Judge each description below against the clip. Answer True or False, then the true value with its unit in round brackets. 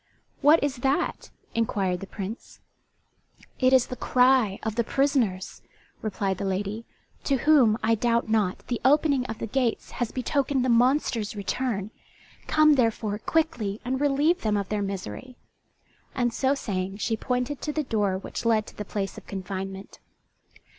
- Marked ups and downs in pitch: False (4.6 semitones)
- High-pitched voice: True (230 Hz)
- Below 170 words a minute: True (160 wpm)